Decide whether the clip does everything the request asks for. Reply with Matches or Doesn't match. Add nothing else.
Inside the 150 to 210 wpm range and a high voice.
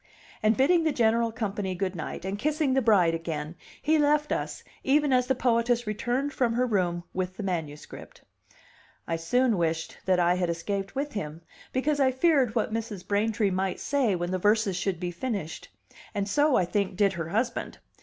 Matches